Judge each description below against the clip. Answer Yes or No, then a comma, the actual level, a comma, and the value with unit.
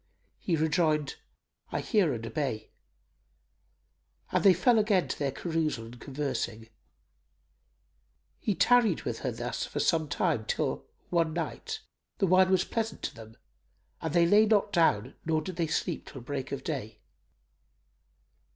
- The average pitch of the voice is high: No, medium, 160 Hz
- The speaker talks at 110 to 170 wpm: Yes, average, 145 wpm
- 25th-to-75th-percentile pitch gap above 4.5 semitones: Yes, average, 5.1 semitones